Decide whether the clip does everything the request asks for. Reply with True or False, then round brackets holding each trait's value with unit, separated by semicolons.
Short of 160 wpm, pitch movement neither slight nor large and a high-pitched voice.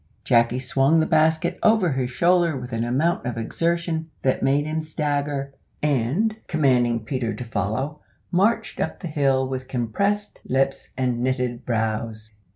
False (150 wpm; 4.6 semitones; 135 Hz)